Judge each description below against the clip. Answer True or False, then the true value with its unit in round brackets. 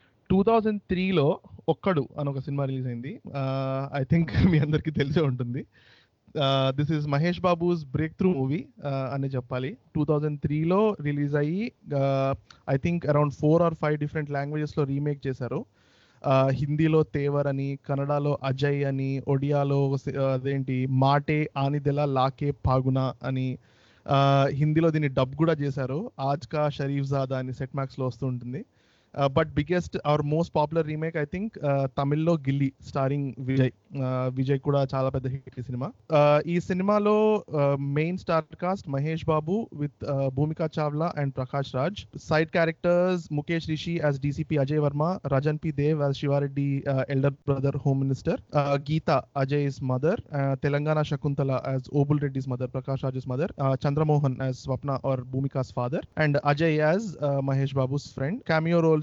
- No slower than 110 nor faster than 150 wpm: True (120 wpm)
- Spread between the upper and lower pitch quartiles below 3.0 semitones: True (2.4 semitones)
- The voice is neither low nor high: True (145 Hz)